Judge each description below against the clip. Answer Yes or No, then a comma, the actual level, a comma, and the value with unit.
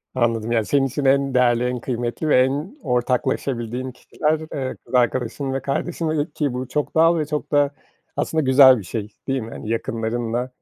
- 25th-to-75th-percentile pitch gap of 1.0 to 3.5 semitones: Yes, average, 3.2 semitones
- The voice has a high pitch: No, low, 130 Hz